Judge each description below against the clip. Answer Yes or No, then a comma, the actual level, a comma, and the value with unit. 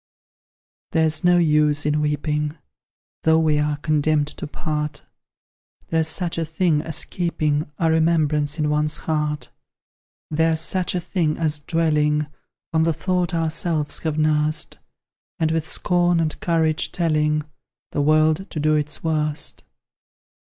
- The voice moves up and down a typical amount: No, narrow, 1.4 semitones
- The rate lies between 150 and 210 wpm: No, slow, 135 wpm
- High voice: No, medium, 155 Hz